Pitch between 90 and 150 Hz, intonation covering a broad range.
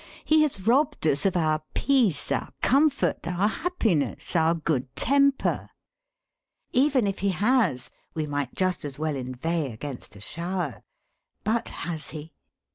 No: medium, 175 Hz; wide, 8.0 semitones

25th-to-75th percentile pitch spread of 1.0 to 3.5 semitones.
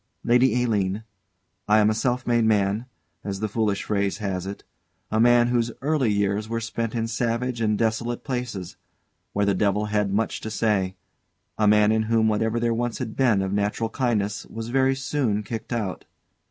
Yes: narrow, 2.5 semitones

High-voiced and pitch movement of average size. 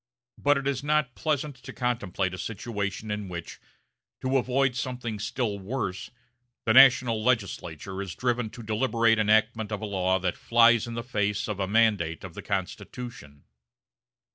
No: low, 110 Hz; average, 4.0 semitones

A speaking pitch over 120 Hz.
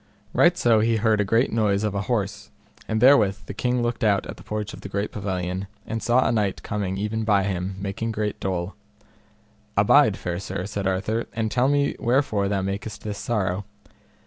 No: low, 105 Hz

